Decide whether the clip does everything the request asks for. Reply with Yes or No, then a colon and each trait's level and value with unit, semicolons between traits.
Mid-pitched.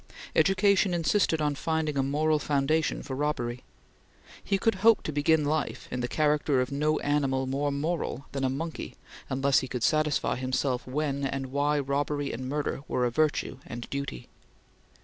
Yes: medium, 145 Hz